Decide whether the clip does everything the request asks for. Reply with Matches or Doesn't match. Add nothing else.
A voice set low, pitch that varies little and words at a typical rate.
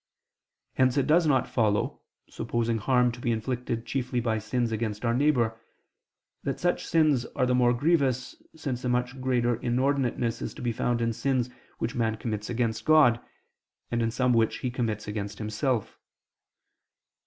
Matches